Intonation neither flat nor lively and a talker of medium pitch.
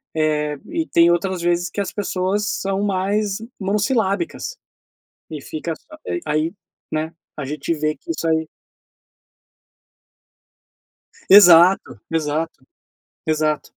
Yes: average, 4.3 semitones; medium, 170 Hz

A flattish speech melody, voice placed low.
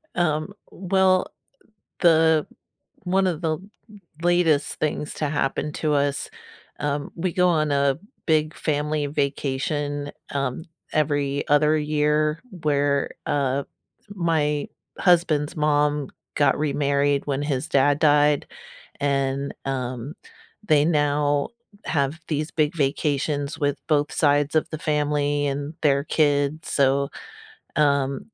No: narrow, 1.5 semitones; medium, 145 Hz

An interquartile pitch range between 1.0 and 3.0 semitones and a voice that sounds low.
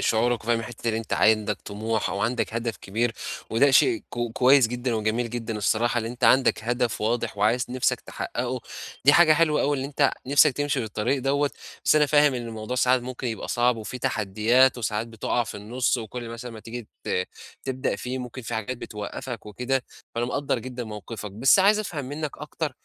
Yes: average, 2.7 semitones; low, 120 Hz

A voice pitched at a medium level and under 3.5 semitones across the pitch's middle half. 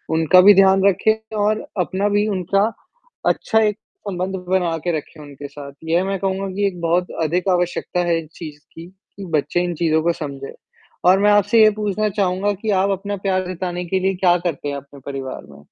Yes: medium, 180 Hz; average, 3.1 semitones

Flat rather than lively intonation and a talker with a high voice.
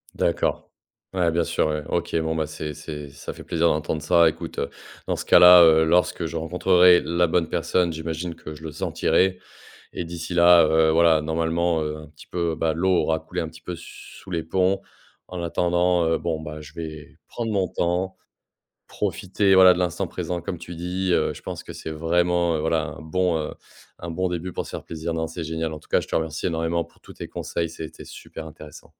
No: narrow, 1.8 semitones; very low, 85 Hz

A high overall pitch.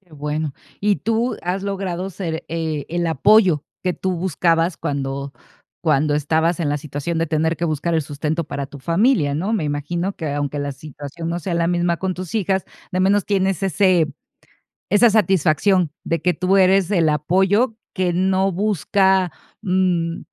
No: medium, 175 Hz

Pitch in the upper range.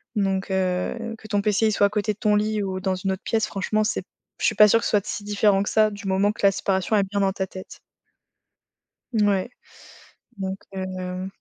Yes: high, 200 Hz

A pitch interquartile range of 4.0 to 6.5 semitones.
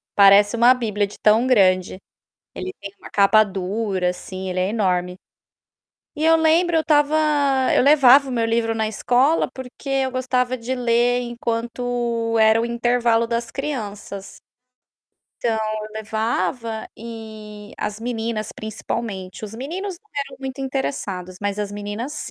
No: average, 3.5 semitones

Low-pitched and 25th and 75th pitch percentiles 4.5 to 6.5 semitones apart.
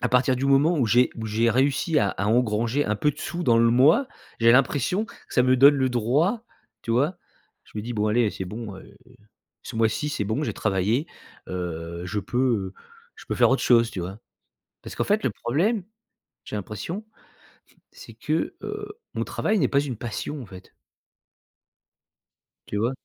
Yes: low, 120 Hz; average, 5.0 semitones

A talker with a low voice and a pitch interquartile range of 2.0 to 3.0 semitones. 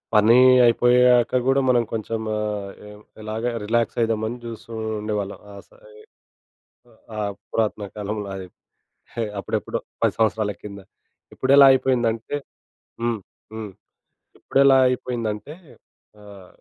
Yes: low, 115 Hz; average, 2.7 semitones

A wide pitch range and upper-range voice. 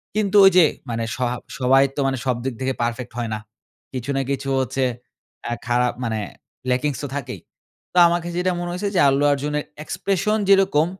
No: wide, 5.7 semitones; low, 135 Hz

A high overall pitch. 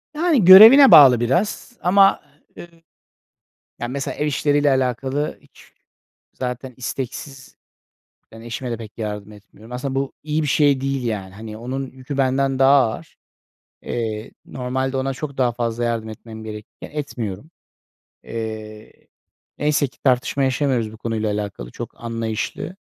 No: low, 130 Hz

